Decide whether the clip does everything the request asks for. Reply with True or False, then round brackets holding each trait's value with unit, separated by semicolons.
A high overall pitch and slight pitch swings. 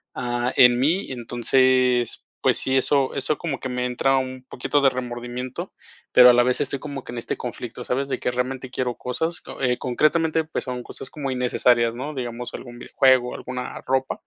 False (125 Hz; 1.5 semitones)